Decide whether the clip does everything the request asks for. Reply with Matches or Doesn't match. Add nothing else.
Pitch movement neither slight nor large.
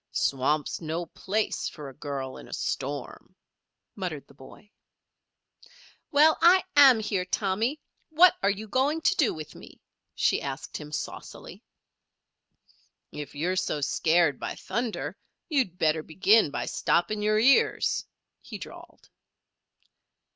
Doesn't match